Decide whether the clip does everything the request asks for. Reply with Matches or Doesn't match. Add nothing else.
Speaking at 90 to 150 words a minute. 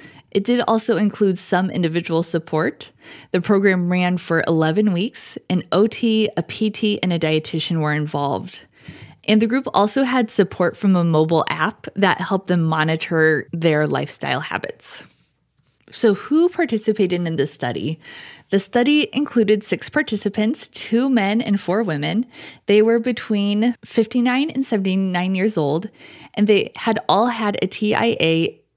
Matches